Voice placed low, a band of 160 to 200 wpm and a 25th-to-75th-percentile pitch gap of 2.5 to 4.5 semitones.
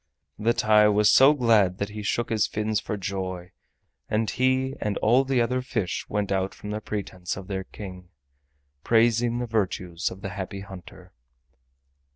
Yes: low, 105 Hz; average, 170 wpm; average, 3.4 semitones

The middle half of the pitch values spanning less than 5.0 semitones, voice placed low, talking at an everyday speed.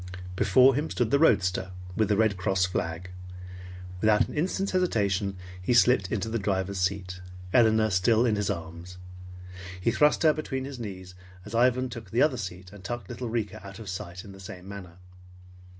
Yes: average, 4.4 semitones; low, 105 Hz; average, 180 wpm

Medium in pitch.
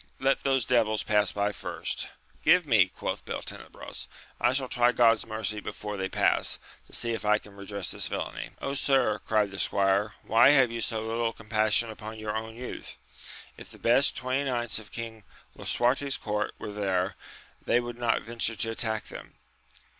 No: low, 110 Hz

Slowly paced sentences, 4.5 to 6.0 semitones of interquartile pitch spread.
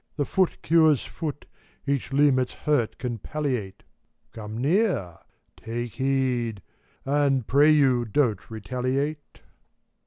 No: slow, 115 wpm; average, 3.8 semitones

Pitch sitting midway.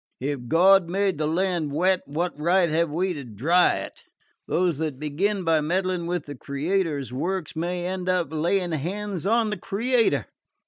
Yes: medium, 175 Hz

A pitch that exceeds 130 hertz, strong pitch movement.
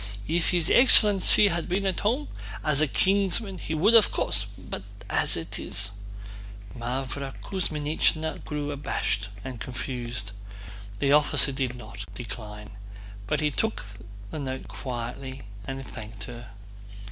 Yes: medium, 140 Hz; wide, 6.2 semitones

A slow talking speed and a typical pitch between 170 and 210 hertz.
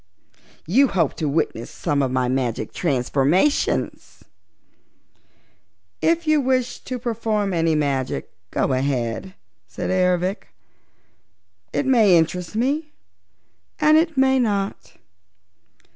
Yes: slow, 105 wpm; medium, 185 Hz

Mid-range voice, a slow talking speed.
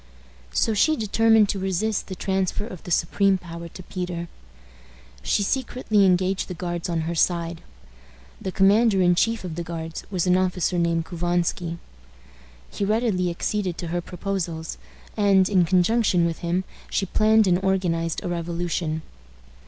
No: medium, 180 Hz; average, 150 wpm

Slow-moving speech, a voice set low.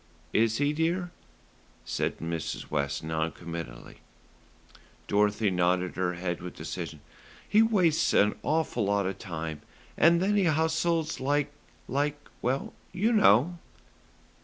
Yes: slow, 125 wpm; low, 120 Hz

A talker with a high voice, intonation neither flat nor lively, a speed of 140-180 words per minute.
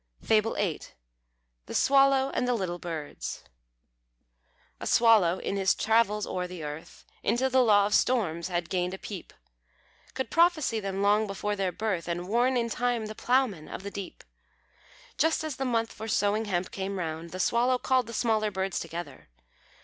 Yes: high, 210 Hz; average, 4.7 semitones; average, 170 wpm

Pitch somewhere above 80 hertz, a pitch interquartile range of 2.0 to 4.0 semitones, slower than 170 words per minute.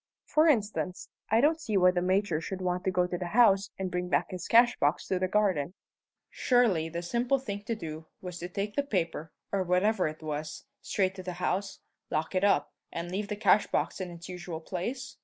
No: medium, 185 Hz; average, 3.0 semitones; average, 200 wpm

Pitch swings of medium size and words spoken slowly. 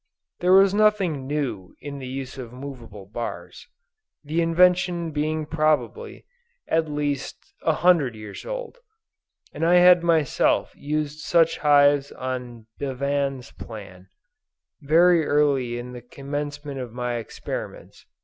Yes: average, 4.4 semitones; slow, 125 wpm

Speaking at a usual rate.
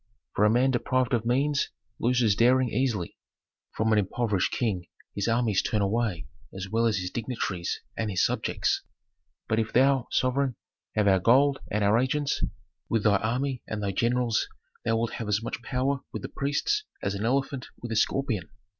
Yes: average, 180 wpm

